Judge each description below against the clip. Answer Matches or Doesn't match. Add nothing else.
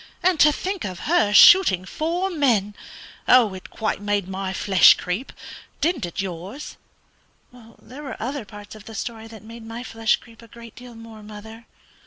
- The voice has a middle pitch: Doesn't match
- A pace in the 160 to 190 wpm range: Matches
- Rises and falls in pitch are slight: Doesn't match